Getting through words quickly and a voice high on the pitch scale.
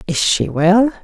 No: average, 175 wpm; high, 200 Hz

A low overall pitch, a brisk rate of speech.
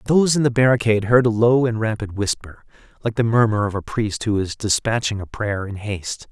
Yes: low, 110 Hz; fast, 220 wpm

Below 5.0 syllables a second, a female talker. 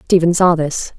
Yes: 4.6 syllables/s; female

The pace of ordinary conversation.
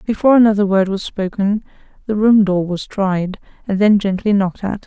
Yes: average, 185 wpm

